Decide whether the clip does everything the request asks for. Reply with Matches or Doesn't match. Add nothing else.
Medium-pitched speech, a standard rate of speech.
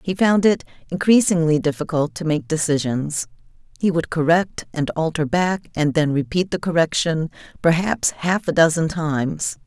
Matches